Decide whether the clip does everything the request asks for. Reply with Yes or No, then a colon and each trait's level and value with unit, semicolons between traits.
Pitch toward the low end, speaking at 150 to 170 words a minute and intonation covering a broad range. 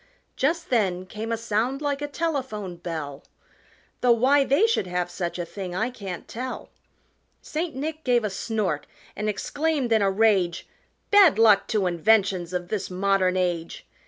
No: high, 215 Hz; average, 160 wpm; wide, 6.3 semitones